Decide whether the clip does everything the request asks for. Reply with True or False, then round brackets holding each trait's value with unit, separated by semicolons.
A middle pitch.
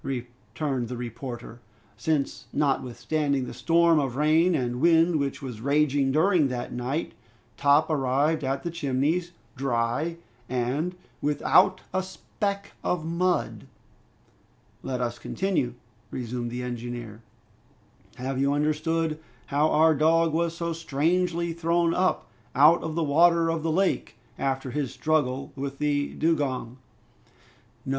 True (145 Hz)